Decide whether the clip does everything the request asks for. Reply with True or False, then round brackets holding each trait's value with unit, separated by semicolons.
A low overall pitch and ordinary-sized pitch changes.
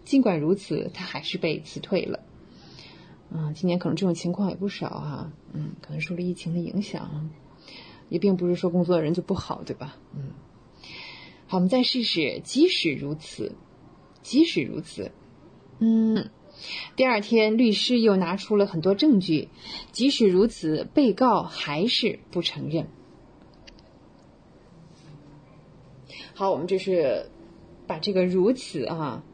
False (185 Hz; 4.6 semitones)